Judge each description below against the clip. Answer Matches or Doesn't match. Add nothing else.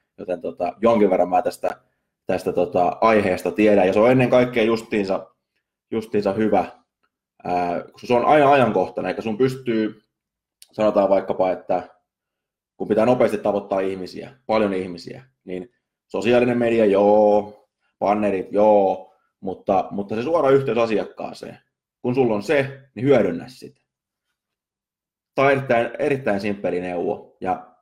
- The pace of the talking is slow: Doesn't match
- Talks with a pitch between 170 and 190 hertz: Doesn't match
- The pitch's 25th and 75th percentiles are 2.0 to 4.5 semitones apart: Matches